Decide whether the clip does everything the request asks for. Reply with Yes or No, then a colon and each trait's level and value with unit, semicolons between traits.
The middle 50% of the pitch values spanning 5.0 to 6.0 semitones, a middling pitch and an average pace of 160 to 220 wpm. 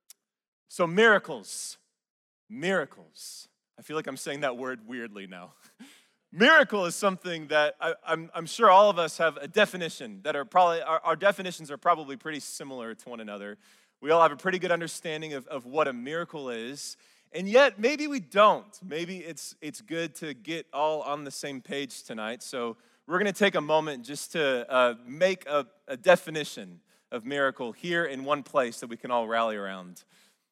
Yes: wide, 5.4 semitones; medium, 160 Hz; average, 185 wpm